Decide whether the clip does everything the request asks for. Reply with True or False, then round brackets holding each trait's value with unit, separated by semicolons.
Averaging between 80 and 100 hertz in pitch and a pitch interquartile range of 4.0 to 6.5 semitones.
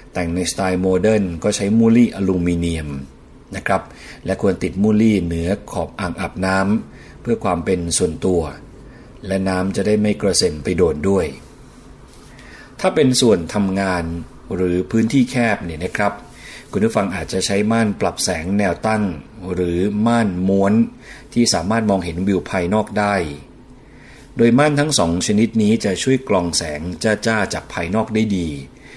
False (95 Hz; 3.6 semitones)